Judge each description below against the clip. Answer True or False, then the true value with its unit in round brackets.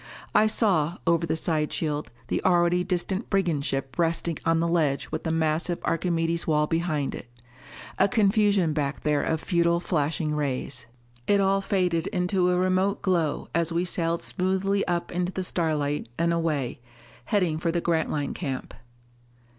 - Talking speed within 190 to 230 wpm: False (160 wpm)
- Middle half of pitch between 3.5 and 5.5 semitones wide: False (2.8 semitones)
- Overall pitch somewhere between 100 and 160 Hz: False (170 Hz)